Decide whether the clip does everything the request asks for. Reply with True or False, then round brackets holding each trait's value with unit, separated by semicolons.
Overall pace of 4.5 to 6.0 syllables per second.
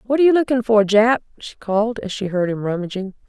False (6.4 syllables/s)